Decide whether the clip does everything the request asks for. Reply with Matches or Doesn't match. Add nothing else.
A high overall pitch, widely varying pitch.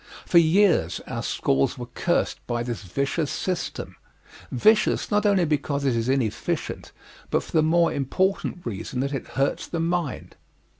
Doesn't match